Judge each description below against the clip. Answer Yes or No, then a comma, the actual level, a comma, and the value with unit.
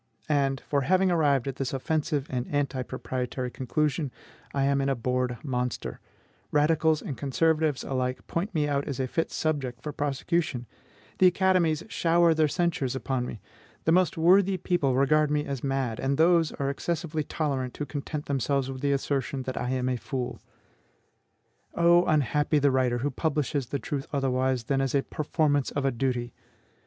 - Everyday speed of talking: Yes, average, 170 wpm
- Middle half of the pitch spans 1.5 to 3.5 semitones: Yes, average, 3.1 semitones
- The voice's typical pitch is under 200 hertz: Yes, medium, 140 Hz